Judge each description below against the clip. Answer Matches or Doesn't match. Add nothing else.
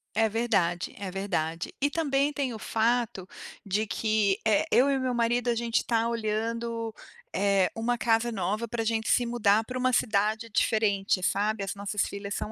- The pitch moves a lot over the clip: Doesn't match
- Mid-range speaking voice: Doesn't match